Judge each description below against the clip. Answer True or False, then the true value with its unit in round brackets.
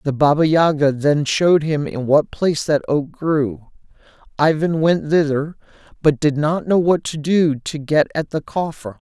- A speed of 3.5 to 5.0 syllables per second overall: True (4.5 syllables/s)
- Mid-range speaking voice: True (150 Hz)